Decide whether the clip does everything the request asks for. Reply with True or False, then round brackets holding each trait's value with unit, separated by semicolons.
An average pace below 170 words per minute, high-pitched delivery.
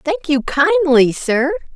True (135 wpm; 255 Hz)